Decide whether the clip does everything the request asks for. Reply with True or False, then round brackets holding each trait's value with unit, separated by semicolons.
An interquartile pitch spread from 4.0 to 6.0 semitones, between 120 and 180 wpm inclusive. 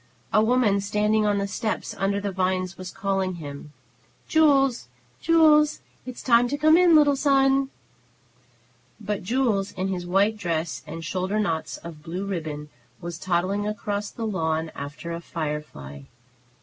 True (5.4 semitones; 150 wpm)